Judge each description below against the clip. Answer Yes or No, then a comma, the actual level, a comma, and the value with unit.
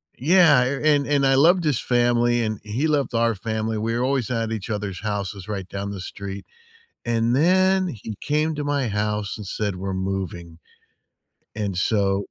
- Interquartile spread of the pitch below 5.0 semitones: No, wide, 5.5 semitones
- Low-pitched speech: Yes, low, 115 Hz